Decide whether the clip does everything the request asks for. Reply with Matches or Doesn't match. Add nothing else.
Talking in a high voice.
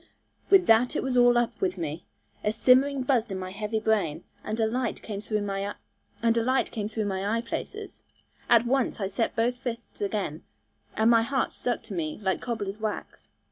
Matches